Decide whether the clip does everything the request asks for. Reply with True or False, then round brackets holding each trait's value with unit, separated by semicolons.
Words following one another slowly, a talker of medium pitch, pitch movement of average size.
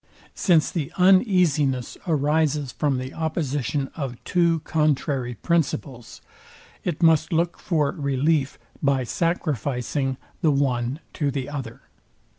True (110 wpm; 145 Hz; 3.4 semitones)